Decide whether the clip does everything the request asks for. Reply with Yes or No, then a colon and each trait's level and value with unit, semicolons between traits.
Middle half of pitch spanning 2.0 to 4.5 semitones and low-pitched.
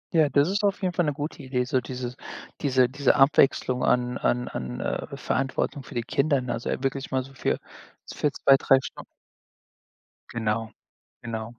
Yes: narrow, 2.5 semitones; low, 130 Hz